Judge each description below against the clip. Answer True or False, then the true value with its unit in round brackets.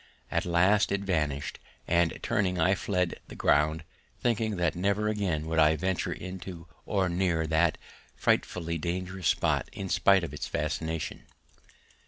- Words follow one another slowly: False (150 wpm)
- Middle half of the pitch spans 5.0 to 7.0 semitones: False (3.0 semitones)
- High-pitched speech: False (90 Hz)